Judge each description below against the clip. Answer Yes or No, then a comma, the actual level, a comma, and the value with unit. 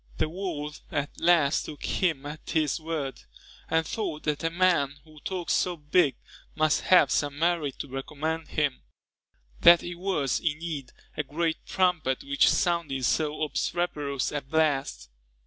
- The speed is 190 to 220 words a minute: No, average, 145 wpm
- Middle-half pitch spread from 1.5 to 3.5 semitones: Yes, average, 3.1 semitones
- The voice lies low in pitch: No, medium, 155 Hz